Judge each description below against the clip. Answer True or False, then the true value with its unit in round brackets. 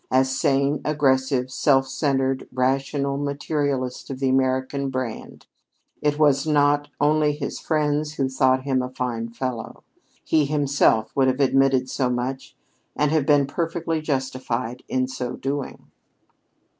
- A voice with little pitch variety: True (2.0 semitones)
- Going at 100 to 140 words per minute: True (135 wpm)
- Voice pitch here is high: False (135 Hz)